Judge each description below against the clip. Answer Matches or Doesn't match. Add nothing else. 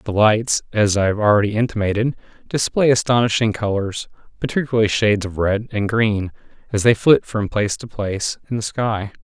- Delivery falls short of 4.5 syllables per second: Doesn't match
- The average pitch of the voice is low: Matches